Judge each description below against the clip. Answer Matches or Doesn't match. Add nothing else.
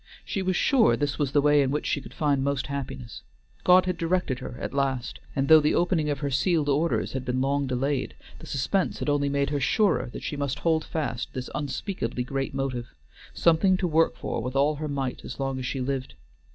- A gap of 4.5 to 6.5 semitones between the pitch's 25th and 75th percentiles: Doesn't match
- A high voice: Doesn't match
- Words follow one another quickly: Matches